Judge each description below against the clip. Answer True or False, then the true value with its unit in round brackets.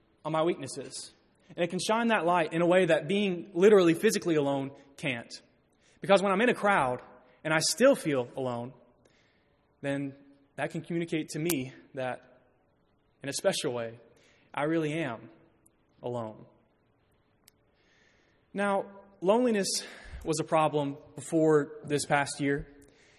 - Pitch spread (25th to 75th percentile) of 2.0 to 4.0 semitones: False (4.7 semitones)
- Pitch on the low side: False (150 Hz)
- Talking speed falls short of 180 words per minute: True (135 wpm)